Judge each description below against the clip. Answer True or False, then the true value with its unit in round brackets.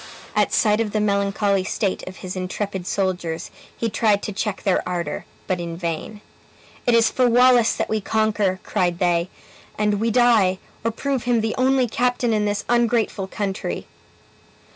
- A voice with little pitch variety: False (3.5 semitones)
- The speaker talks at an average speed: True (165 wpm)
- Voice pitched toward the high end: True (210 Hz)